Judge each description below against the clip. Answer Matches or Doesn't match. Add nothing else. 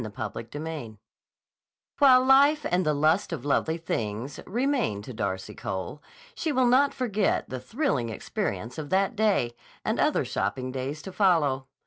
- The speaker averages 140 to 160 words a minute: Matches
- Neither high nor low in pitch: Matches